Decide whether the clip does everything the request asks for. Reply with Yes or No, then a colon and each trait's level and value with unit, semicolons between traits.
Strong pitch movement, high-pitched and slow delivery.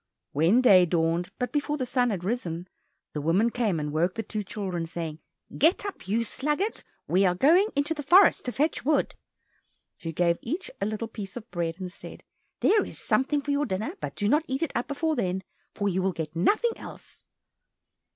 No: wide, 8.3 semitones; high, 215 Hz; average, 200 wpm